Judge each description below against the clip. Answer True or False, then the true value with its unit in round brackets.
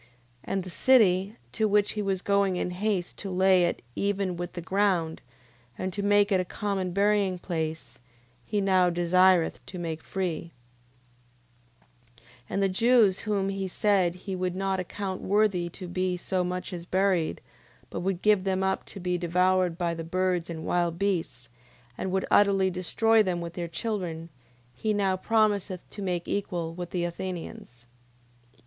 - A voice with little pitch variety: True (2.1 semitones)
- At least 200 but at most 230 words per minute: False (170 wpm)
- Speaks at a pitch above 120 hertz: True (185 Hz)